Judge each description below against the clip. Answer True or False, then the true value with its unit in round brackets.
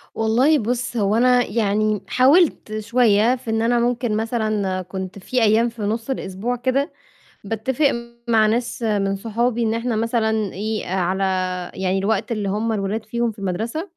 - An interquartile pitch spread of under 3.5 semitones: True (2.7 semitones)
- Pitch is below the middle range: False (220 Hz)